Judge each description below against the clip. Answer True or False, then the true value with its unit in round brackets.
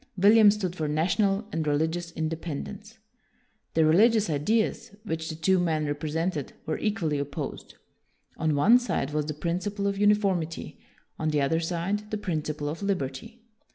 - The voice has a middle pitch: True (165 Hz)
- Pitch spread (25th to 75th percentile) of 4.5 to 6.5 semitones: True (4.8 semitones)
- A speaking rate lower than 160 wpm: True (150 wpm)